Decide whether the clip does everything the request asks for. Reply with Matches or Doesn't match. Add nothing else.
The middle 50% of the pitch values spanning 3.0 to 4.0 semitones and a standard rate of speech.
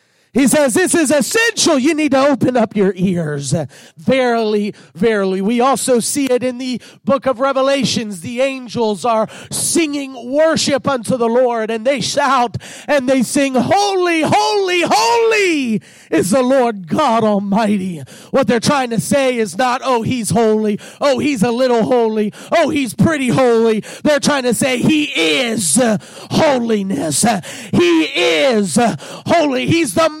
Doesn't match